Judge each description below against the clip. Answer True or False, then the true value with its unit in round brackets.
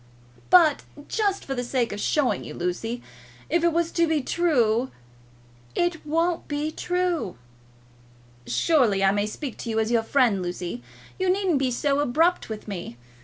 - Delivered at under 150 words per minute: False (165 wpm)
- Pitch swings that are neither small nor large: False (7.2 semitones)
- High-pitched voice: True (275 Hz)